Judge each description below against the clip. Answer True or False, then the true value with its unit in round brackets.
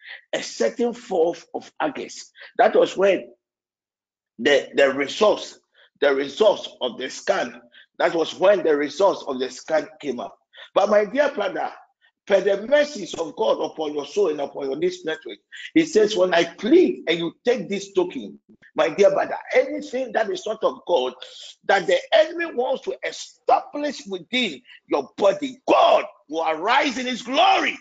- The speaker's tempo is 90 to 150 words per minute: False (170 wpm)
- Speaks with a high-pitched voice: True (260 Hz)